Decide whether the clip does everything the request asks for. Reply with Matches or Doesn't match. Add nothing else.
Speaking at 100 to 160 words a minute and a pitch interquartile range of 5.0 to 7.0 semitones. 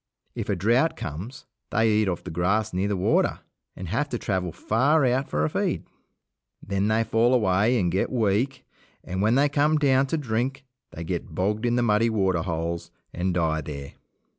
Doesn't match